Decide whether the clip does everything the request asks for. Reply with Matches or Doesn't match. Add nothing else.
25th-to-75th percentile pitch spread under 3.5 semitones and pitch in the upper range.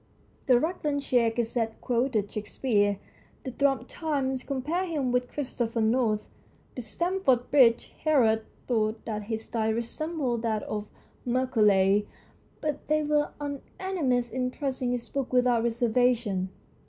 Doesn't match